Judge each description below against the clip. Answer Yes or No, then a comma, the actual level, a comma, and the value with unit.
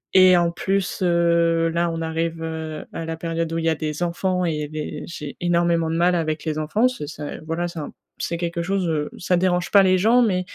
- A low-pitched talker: No, medium, 170 Hz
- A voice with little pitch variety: Yes, narrow, 1.7 semitones